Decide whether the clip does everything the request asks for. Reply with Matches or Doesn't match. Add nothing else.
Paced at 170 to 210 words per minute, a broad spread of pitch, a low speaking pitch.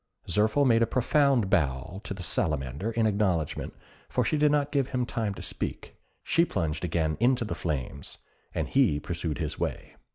Matches